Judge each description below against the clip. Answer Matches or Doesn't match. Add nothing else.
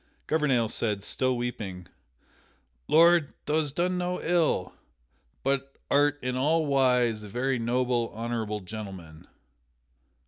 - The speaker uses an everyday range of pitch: Matches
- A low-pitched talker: Matches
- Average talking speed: Doesn't match